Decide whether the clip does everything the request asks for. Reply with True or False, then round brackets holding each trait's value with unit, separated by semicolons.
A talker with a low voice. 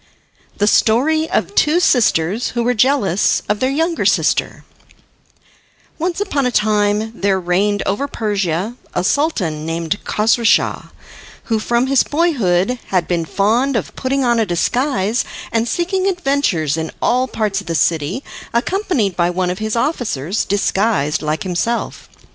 False (220 Hz)